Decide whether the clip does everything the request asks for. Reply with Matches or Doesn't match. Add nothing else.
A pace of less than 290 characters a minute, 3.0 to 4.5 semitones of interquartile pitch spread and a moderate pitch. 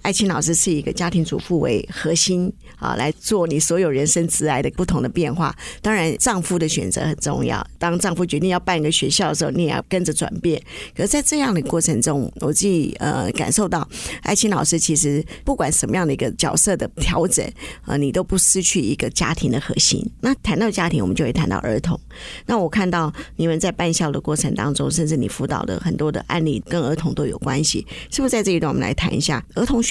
Doesn't match